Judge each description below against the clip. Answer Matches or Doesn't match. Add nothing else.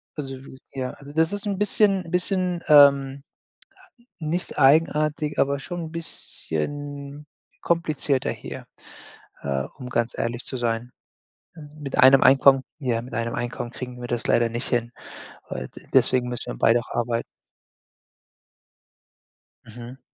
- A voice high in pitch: Doesn't match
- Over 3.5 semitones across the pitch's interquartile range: Matches